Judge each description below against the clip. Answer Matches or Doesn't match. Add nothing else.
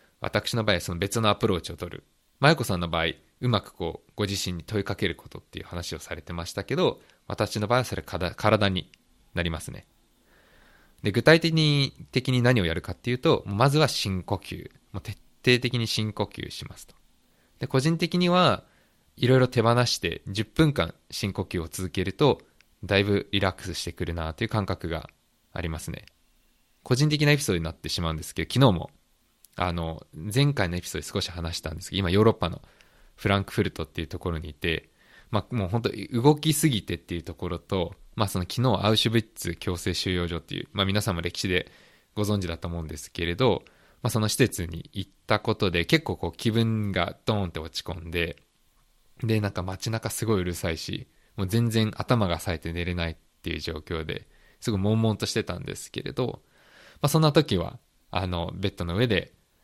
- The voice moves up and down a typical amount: Matches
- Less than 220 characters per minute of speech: Doesn't match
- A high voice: Doesn't match